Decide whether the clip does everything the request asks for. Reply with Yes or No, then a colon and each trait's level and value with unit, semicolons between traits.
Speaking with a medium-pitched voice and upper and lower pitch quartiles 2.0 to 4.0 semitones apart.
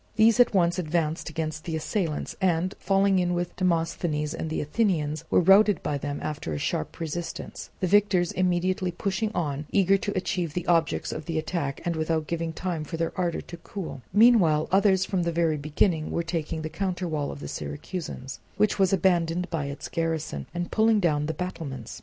Yes: medium, 170 Hz; average, 3.1 semitones